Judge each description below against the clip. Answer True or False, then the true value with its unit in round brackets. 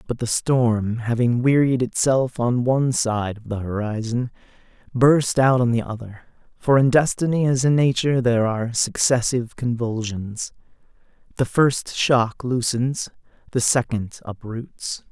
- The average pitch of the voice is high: False (120 Hz)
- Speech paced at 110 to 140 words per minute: True (135 wpm)